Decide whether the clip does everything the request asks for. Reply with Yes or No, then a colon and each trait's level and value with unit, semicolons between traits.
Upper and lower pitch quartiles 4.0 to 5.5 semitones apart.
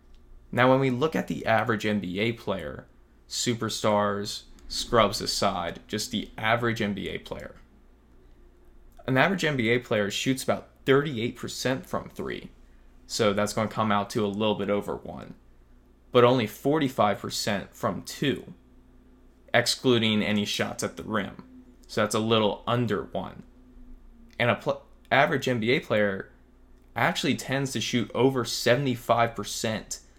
No: average, 3.3 semitones